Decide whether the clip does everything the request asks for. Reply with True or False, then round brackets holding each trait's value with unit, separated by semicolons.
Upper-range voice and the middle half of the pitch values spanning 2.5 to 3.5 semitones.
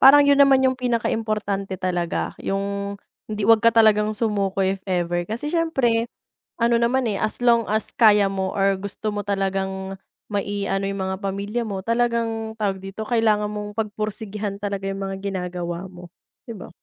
True (205 Hz; 2.8 semitones)